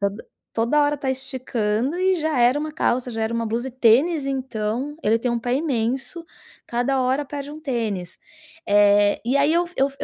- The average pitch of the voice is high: Yes, very high, 255 Hz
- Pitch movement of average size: Yes, average, 4.2 semitones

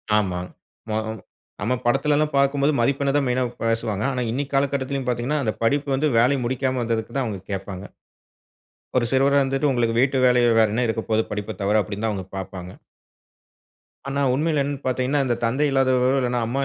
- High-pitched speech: No, low, 125 Hz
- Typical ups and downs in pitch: Yes, average, 3.5 semitones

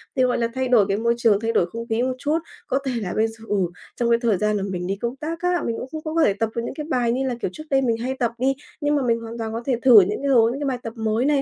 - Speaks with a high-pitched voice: Yes, high, 235 Hz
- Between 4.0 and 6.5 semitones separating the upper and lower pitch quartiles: No, average, 3.2 semitones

